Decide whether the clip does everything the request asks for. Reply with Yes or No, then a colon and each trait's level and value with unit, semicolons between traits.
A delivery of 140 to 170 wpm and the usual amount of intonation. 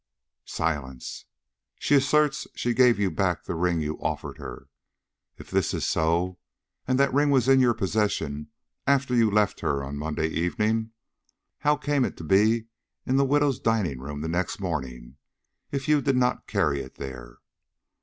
No: average, 165 wpm; wide, 8.9 semitones